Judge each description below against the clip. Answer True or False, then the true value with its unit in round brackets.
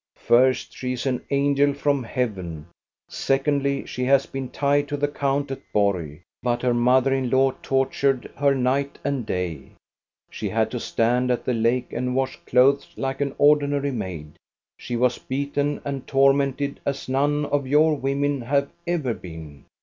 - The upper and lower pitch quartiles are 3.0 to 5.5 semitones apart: False (2.4 semitones)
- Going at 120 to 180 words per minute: True (165 wpm)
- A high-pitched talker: False (135 Hz)